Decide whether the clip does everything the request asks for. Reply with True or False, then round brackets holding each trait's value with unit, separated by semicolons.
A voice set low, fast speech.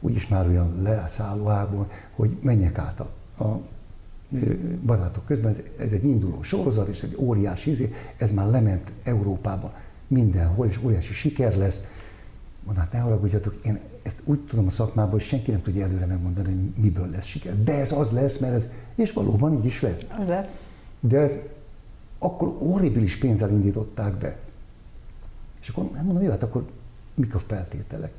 True (110 Hz; 165 wpm)